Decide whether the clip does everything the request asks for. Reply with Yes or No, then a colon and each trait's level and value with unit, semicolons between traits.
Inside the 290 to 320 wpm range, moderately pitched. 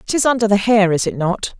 No: fast, 300 wpm; high, 210 Hz